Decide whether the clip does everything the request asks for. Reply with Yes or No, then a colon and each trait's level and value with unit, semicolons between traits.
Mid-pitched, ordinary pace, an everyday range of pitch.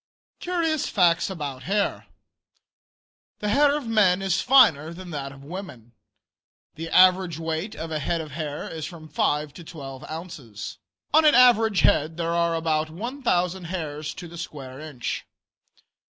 Yes: medium, 165 Hz; average, 150 wpm; average, 4.1 semitones